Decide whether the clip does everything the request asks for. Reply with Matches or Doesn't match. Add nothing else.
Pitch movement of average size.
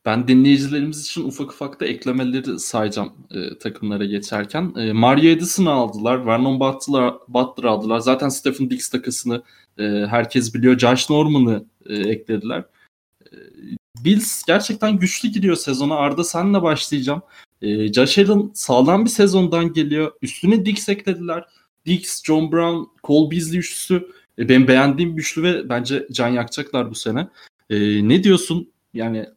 Doesn't match